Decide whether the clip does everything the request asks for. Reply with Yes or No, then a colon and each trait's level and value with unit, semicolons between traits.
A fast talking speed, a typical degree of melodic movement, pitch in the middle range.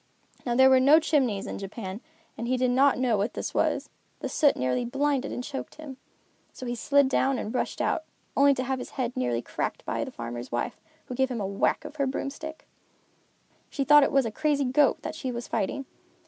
No: fast, 220 wpm; average, 3.2 semitones; very high, 260 Hz